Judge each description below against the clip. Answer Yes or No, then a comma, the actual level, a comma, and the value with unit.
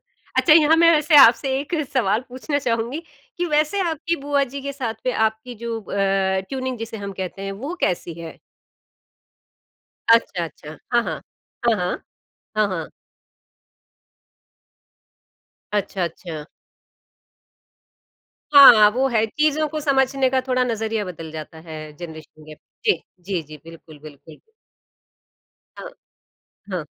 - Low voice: No, high, 225 Hz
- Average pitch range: No, wide, 7.5 semitones